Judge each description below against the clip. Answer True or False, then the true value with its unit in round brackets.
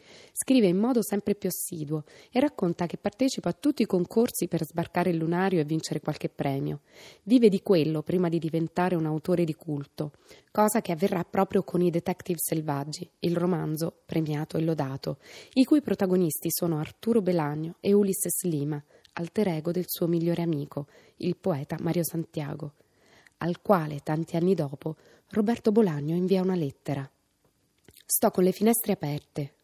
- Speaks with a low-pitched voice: False (175 Hz)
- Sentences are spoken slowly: False (160 wpm)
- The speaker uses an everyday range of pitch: True (3.6 semitones)